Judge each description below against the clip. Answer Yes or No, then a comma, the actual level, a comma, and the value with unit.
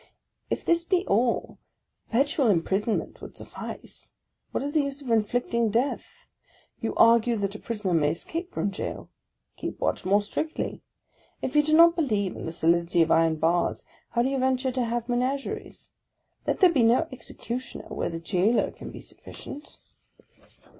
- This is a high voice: Yes, high, 235 Hz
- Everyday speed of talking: Yes, average, 165 wpm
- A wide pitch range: Yes, wide, 5.8 semitones